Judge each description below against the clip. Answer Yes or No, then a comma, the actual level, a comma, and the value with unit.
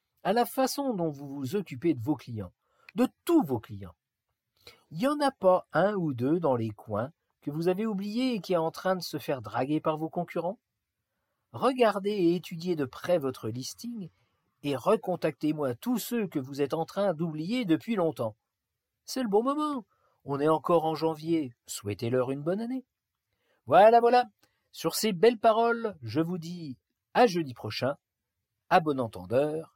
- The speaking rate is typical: Yes, average, 175 wpm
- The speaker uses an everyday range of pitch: No, wide, 8.0 semitones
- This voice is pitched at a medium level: Yes, medium, 165 Hz